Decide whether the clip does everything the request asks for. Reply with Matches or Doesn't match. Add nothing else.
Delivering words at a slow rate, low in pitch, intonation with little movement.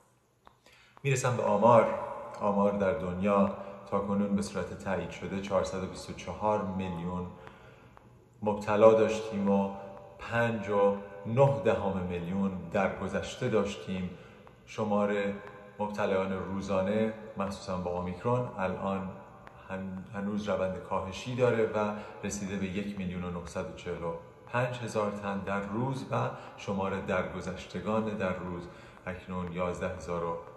Matches